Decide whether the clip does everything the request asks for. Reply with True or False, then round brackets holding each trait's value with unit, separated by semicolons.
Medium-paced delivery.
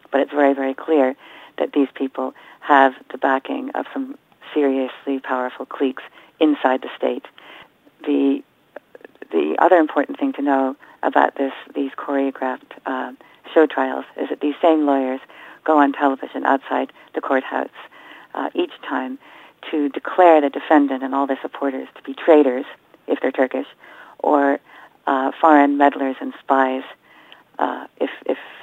True (145 wpm)